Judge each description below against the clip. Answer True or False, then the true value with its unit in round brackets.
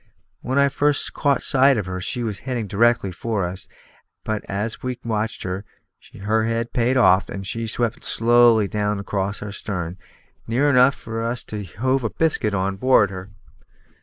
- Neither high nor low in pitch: False (110 Hz)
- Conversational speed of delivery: True (180 wpm)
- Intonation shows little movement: False (3.6 semitones)